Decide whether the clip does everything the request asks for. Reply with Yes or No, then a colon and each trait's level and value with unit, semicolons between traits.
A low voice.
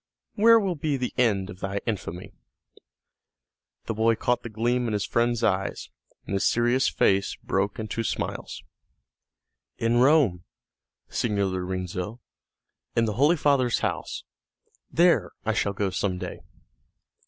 Yes: low, 115 Hz